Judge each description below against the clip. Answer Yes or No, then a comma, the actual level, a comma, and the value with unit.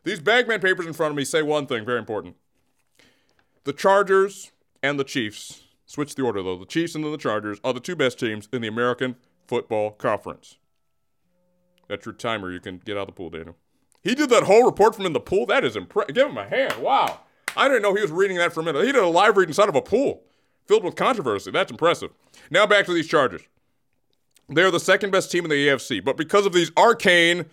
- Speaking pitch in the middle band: Yes, medium, 155 Hz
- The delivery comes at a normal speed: No, fast, 235 wpm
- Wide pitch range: Yes, wide, 7.3 semitones